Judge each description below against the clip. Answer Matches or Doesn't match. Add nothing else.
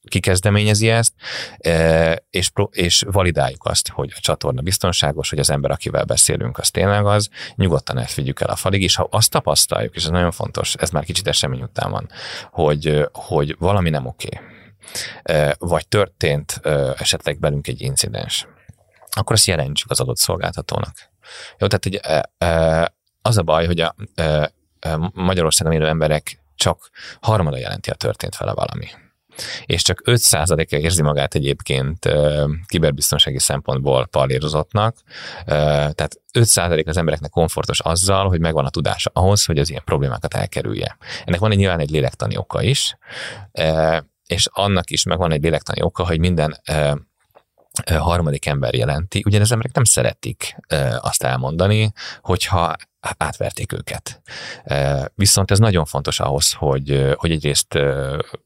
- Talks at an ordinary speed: Matches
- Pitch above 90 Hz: Doesn't match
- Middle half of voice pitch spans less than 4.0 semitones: Doesn't match